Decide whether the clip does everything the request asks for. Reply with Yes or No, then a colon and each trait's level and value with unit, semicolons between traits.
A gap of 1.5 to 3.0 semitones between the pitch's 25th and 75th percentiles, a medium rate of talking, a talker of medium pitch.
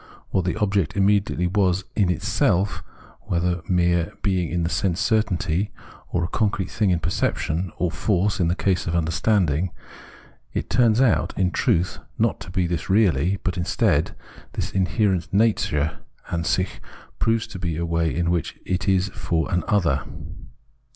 No: average, 2.7 semitones; average, 155 wpm; very low, 90 Hz